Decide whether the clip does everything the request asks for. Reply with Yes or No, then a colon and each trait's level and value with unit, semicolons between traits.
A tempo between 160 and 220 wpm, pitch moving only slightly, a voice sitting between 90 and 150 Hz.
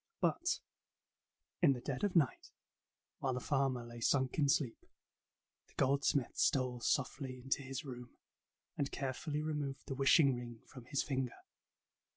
No: average, 145 wpm; narrow, 2.0 semitones; low, 135 Hz